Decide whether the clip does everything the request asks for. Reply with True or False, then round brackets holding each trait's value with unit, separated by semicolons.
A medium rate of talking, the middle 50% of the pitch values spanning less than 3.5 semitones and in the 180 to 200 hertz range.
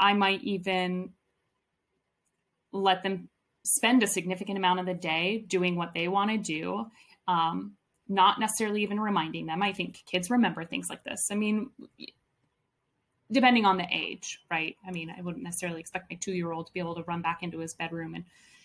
True (185 wpm; 3.1 semitones; 185 Hz)